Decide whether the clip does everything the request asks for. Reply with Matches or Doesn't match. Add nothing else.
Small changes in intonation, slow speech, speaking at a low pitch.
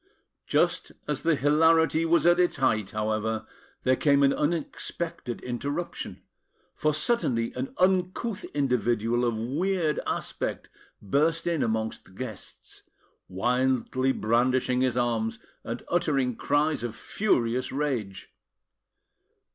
Doesn't match